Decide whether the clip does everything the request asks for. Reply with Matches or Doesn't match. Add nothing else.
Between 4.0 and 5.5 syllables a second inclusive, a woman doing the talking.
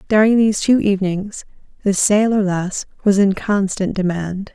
Matches